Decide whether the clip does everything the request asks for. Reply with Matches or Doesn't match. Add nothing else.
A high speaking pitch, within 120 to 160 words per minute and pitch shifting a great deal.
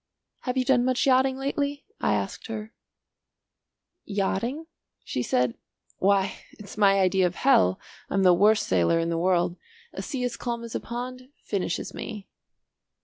Matches